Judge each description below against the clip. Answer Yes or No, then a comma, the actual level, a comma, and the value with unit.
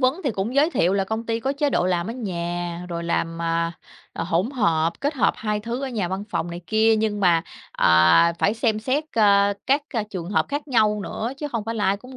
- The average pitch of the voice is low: No, high, 210 Hz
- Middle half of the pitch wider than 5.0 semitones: Yes, wide, 5.4 semitones